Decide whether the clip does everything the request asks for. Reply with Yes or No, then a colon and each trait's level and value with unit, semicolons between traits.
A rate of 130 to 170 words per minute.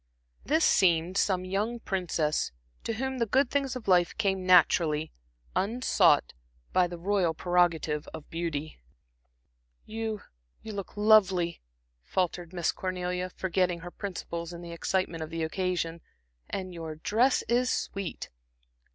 Yes: slow, 135 wpm